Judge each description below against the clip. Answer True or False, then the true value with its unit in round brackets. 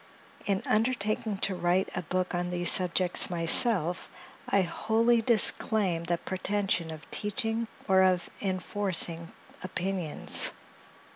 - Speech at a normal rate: False (115 wpm)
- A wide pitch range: False (2.9 semitones)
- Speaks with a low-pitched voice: False (185 Hz)